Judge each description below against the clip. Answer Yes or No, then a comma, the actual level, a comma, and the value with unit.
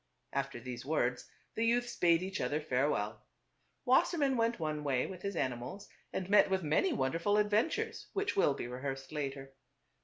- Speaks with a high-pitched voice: No, medium, 165 Hz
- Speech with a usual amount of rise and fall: No, wide, 7.7 semitones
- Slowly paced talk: No, average, 165 wpm